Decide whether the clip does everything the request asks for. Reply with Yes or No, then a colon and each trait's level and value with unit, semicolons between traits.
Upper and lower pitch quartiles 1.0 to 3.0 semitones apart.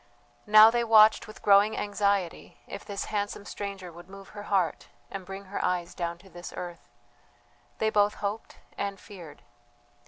Yes: narrow, 2.4 semitones